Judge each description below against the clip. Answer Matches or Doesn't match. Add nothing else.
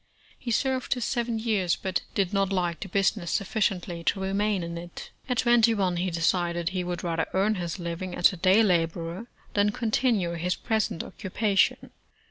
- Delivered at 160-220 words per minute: Matches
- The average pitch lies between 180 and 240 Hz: Matches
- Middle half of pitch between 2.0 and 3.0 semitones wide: Doesn't match